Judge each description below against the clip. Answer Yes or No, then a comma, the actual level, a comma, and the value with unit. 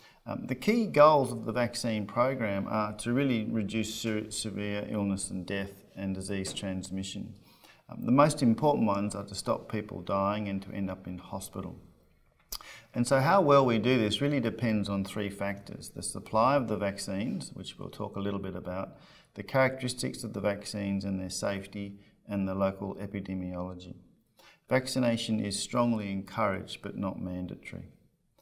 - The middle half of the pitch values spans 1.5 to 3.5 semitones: Yes, average, 2.9 semitones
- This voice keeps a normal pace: Yes, average, 165 wpm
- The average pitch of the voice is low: Yes, low, 105 Hz